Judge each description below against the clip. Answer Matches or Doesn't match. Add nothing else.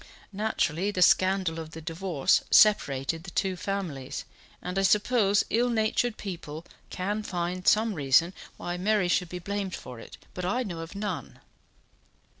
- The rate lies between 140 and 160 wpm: Matches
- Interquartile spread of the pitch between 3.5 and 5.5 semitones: Matches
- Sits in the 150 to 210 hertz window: Matches